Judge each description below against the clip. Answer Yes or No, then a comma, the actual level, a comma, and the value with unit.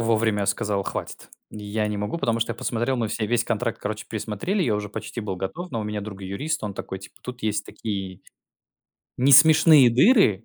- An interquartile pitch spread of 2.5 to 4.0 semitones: Yes, average, 3.0 semitones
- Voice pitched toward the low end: Yes, low, 110 Hz